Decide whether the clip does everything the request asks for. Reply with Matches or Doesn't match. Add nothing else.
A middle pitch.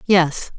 Matches